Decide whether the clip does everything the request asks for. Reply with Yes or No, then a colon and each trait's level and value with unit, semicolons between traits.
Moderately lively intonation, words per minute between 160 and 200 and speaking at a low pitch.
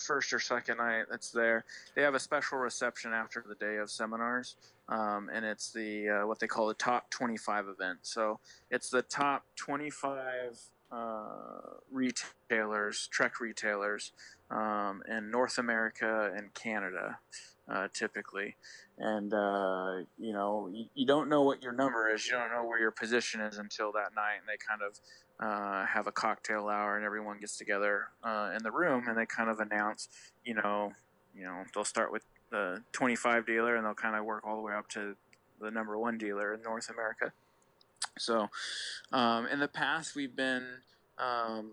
No: narrow, 2.1 semitones; average, 180 wpm; low, 110 Hz